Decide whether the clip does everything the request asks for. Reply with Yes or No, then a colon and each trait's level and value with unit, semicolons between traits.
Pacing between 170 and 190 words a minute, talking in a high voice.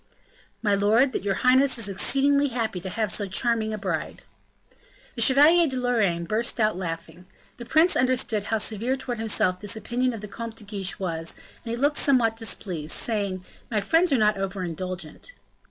Yes: average, 185 wpm; high, 220 Hz